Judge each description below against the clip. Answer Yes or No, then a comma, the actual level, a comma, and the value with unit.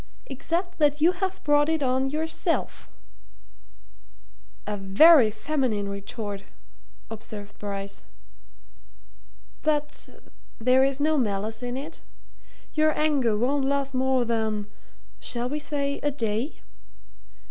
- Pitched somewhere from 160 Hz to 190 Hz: No, very high, 265 Hz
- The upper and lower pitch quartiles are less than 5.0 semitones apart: No, wide, 5.4 semitones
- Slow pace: Yes, slow, 110 wpm